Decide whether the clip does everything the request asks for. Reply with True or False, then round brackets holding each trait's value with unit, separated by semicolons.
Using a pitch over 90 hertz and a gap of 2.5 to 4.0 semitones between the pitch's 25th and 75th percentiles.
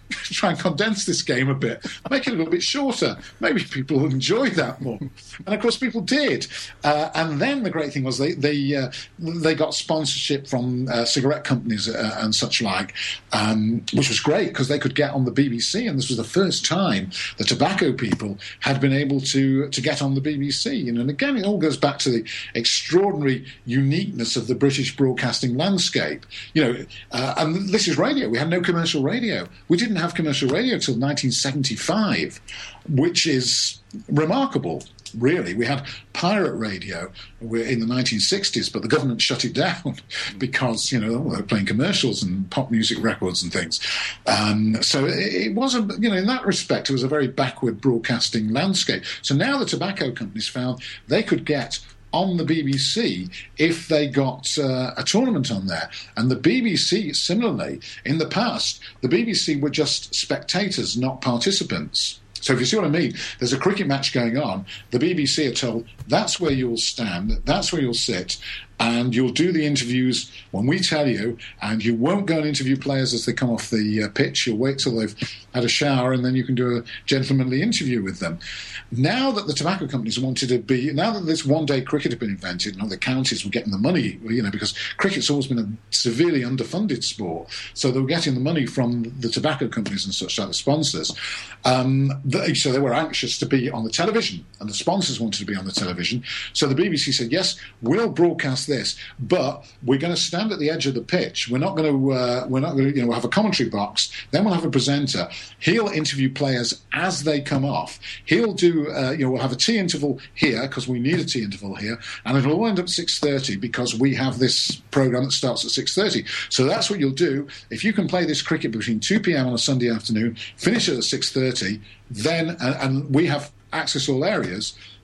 False (135 Hz; 4.8 semitones)